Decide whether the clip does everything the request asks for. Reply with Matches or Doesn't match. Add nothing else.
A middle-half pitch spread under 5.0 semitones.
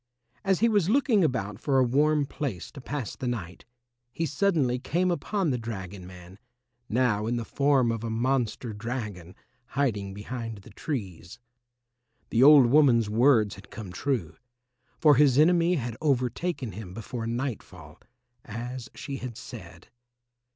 Doesn't match